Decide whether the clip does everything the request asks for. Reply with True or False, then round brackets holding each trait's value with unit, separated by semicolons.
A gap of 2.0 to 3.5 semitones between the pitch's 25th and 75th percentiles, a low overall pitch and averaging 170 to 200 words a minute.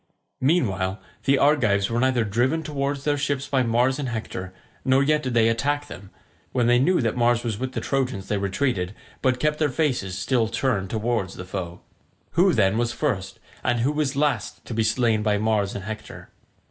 False (4.8 semitones; 120 Hz; 190 wpm)